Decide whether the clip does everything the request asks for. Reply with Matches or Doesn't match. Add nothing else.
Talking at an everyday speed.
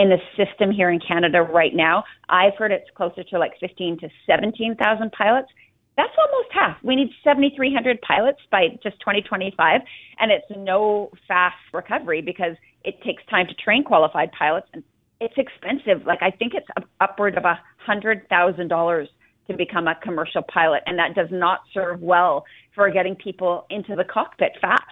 Matches